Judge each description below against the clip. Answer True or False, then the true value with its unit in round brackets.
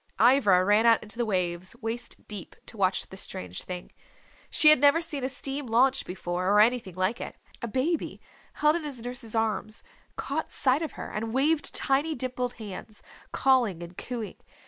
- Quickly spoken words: False (180 wpm)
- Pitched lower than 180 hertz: False (230 Hz)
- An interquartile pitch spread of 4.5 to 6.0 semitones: True (5.2 semitones)